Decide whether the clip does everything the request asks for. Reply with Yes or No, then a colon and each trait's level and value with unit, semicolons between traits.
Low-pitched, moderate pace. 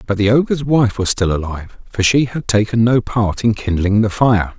No: low, 110 Hz; fast, 220 wpm